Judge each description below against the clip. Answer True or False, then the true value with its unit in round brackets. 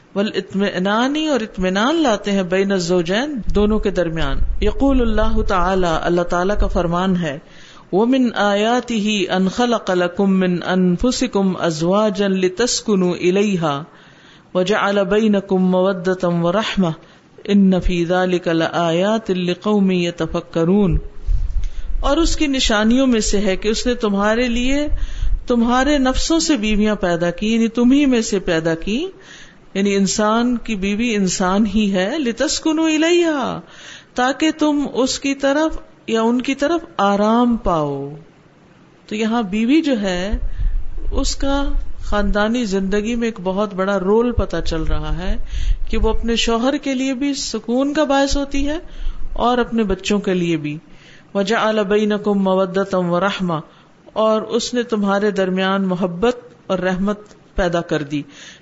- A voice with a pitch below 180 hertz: False (205 Hz)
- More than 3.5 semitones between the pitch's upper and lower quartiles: True (4.6 semitones)